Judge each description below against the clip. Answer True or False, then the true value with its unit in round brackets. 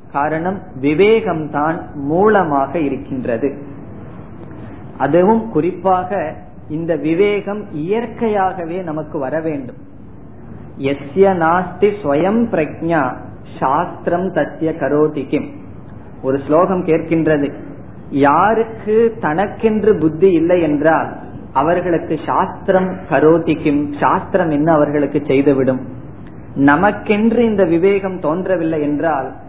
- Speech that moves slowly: True (65 wpm)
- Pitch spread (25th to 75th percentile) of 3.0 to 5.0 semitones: True (4.5 semitones)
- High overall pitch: False (160 Hz)